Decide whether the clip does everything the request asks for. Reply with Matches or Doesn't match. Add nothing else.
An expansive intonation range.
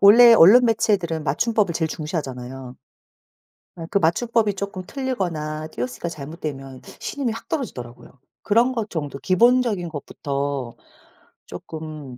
Matches